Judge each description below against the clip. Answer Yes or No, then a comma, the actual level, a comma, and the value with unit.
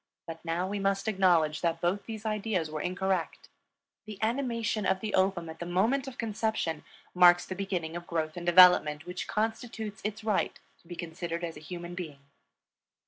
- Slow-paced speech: No, average, 180 wpm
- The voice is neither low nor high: Yes, medium, 180 Hz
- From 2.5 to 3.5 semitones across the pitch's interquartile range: No, average, 3.9 semitones